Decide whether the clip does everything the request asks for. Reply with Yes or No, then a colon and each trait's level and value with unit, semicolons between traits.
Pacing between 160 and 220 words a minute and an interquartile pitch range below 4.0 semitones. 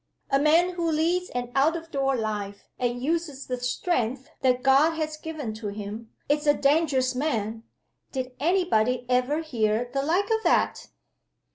No: average, 165 wpm; average, 4.6 semitones